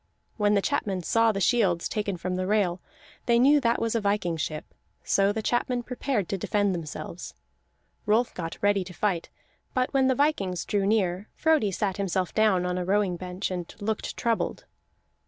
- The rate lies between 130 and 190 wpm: Yes, average, 180 wpm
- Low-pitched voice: No, high, 200 Hz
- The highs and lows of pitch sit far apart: No, average, 3.8 semitones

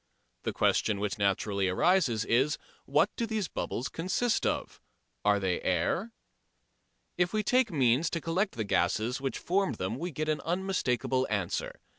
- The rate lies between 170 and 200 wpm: No, average, 155 wpm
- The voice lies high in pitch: No, low, 135 Hz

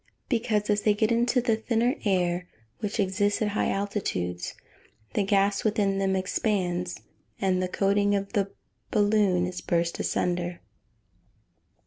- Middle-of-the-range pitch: No, high, 200 Hz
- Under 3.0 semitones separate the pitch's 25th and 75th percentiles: Yes, narrow, 2.6 semitones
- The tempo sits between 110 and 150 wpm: Yes, average, 140 wpm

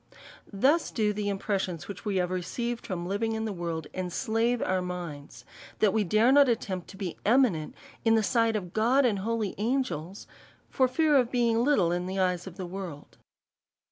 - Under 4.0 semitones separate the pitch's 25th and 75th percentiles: No, average, 4.4 semitones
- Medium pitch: No, high, 205 Hz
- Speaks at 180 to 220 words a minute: Yes, average, 185 wpm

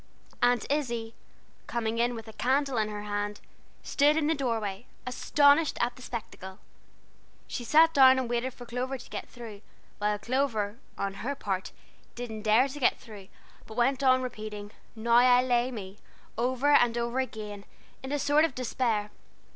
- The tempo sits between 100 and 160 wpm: No, average, 170 wpm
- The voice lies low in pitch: No, high, 240 Hz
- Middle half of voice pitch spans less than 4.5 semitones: Yes, average, 3.4 semitones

